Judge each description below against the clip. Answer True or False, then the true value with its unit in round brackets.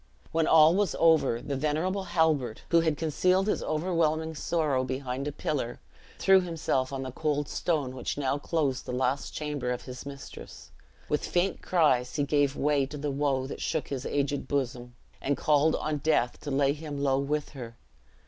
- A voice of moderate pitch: True (145 Hz)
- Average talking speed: True (180 wpm)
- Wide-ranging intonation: False (3.0 semitones)